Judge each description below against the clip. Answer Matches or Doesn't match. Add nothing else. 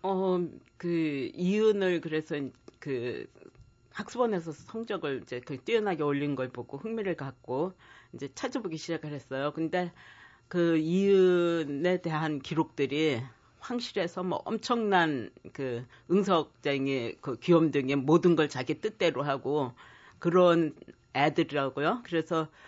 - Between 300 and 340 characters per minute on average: Doesn't match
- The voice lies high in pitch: Doesn't match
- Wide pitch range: Doesn't match